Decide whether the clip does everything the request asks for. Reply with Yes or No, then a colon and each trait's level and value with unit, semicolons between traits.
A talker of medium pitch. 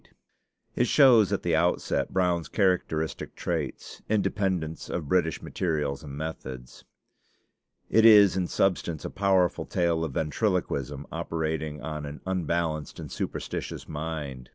No: very low, 80 Hz